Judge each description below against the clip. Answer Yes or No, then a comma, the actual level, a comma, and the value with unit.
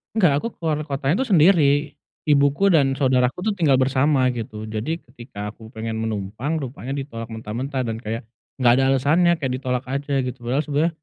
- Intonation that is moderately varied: Yes, average, 4.0 semitones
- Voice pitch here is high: No, low, 135 Hz